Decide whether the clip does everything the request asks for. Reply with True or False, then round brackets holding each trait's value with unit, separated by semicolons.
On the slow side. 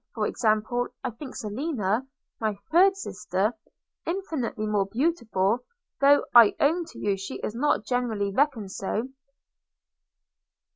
True (125 wpm)